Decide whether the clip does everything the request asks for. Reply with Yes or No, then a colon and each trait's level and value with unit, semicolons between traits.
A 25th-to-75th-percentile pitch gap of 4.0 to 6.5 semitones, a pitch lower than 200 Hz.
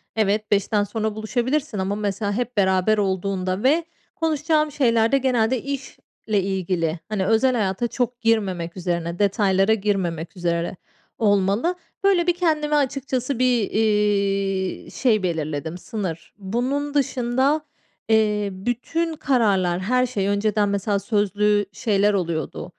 No: average, 4.6 semitones; high, 210 Hz